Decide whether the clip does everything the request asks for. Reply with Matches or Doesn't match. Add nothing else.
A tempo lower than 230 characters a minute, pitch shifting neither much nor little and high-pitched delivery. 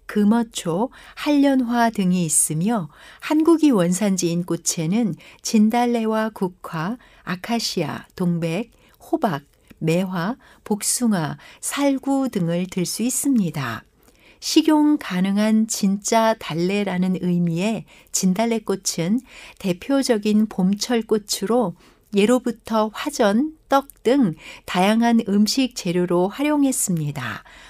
Matches